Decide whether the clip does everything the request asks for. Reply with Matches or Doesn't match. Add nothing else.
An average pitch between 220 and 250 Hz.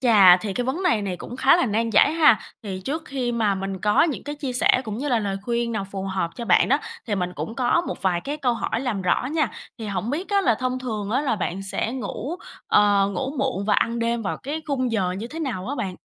Matches